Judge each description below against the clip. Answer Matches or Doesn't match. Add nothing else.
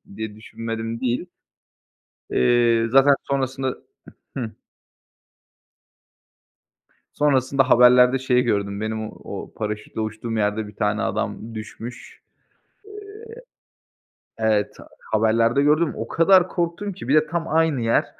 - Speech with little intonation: Doesn't match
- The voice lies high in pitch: Doesn't match